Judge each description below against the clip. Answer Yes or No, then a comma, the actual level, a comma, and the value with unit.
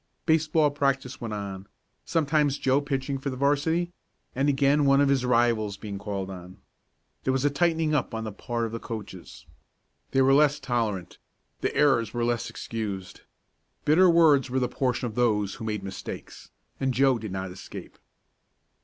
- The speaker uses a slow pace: No, average, 170 wpm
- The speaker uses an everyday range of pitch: Yes, average, 4.8 semitones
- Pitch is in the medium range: No, low, 130 Hz